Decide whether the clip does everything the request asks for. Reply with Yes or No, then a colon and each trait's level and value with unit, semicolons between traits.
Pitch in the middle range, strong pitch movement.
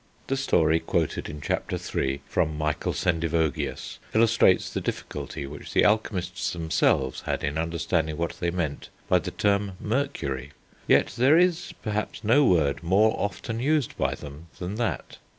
No: very low, 90 Hz; wide, 6.0 semitones